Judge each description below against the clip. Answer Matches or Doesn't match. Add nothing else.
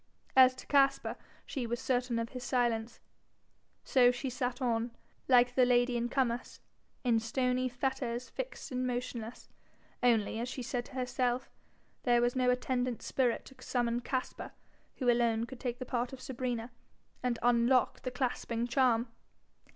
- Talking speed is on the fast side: Doesn't match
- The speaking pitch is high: Matches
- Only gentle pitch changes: Matches